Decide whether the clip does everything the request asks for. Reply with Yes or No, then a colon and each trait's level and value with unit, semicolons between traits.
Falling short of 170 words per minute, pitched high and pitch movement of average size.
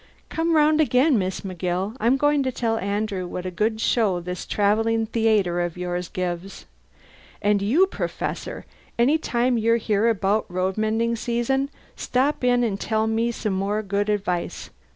Yes: average, 160 wpm; high, 220 Hz; average, 3.6 semitones